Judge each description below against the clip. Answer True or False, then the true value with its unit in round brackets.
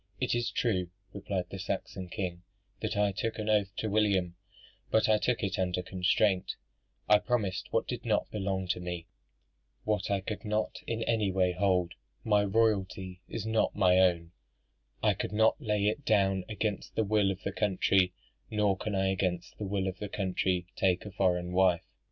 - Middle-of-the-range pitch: False (95 Hz)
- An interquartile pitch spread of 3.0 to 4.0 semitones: False (2.5 semitones)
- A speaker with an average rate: True (180 wpm)